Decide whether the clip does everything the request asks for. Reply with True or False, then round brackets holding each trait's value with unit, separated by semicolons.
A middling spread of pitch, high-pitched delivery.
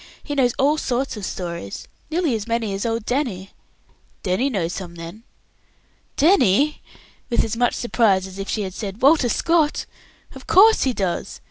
False (6.3 semitones; 230 Hz)